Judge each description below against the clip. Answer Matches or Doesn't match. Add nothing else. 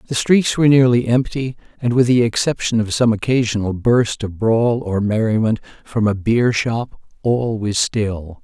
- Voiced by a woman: Doesn't match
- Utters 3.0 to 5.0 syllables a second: Matches